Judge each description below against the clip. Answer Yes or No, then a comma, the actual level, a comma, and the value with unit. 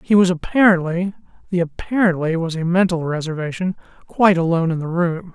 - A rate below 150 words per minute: Yes, slow, 135 wpm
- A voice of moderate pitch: Yes, medium, 175 Hz